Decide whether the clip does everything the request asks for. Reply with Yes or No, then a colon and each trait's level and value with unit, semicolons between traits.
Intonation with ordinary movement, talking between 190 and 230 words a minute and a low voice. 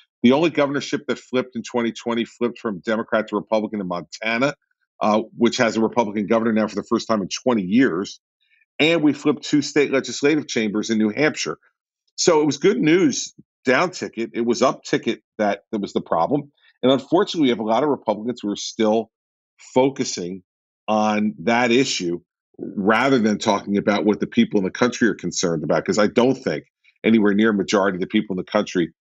Yes: average, 4.0 semitones; average, 200 wpm; low, 115 Hz